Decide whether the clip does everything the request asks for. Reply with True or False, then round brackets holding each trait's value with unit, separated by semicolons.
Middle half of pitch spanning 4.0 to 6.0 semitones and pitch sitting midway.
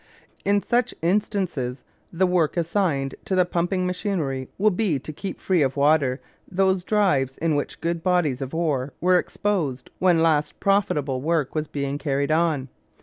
True (4.8 semitones; 165 Hz)